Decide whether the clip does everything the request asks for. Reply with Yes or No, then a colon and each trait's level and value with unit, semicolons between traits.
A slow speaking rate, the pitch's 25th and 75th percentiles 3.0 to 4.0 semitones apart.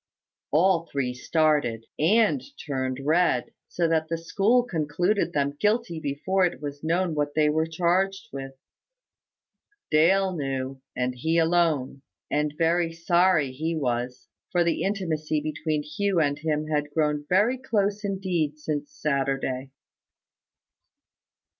Yes: slow, 130 wpm; average, 3.7 semitones